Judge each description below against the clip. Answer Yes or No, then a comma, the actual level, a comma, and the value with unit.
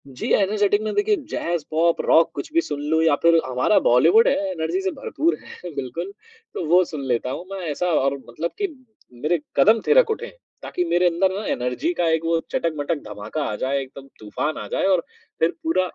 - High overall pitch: No, medium, 170 Hz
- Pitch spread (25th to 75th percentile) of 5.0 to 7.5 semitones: Yes, wide, 5.6 semitones